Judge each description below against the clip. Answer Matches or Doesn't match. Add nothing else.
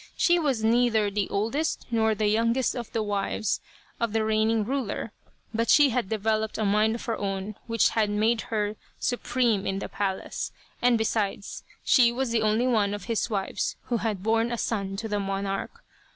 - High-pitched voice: Matches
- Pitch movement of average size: Doesn't match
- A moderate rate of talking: Matches